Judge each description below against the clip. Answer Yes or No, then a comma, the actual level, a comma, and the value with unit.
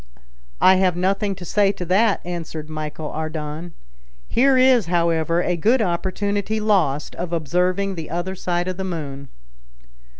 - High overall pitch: No, medium, 180 Hz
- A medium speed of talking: Yes, average, 145 wpm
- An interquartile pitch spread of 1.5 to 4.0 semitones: Yes, average, 3.5 semitones